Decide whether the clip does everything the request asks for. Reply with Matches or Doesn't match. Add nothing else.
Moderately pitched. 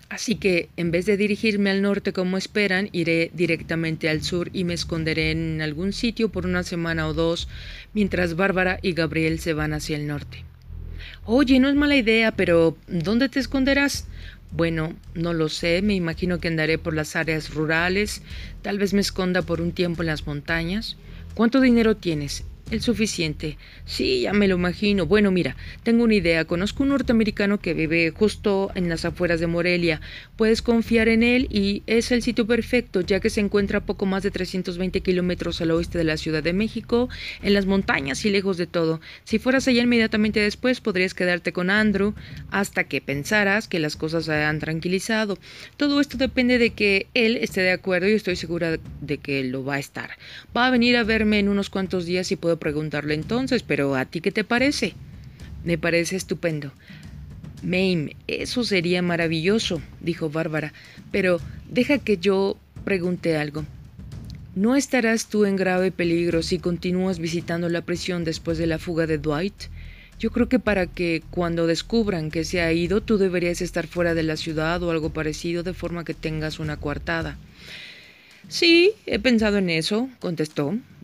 Matches